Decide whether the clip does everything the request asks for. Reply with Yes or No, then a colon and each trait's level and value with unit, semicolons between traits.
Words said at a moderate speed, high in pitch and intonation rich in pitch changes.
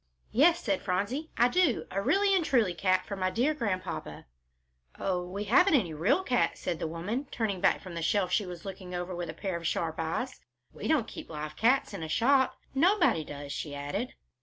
No: fast, 210 wpm; high, 195 Hz; wide, 7.2 semitones